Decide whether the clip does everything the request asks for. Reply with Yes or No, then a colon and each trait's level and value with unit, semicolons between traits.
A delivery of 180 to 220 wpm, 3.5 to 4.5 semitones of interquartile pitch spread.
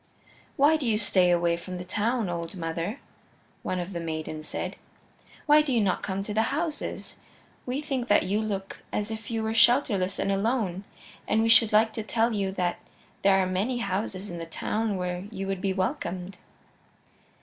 Yes: average, 190 wpm; average, 3.8 semitones